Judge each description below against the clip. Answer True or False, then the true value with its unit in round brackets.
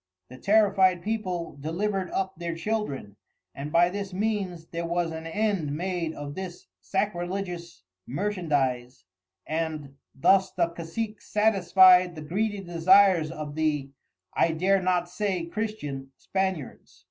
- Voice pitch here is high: False (175 Hz)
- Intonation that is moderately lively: True (3.4 semitones)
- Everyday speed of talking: False (125 wpm)